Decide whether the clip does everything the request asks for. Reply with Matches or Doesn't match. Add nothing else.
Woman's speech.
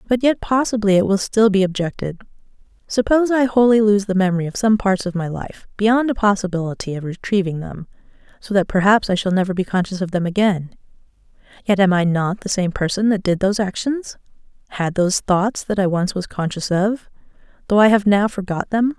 Matches